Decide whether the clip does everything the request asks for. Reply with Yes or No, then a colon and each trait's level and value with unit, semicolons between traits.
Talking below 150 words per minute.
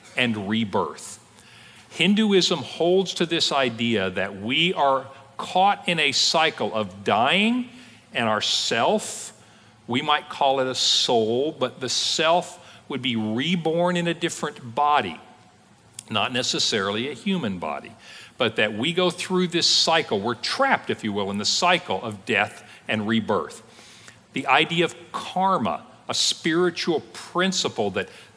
Yes: average, 140 wpm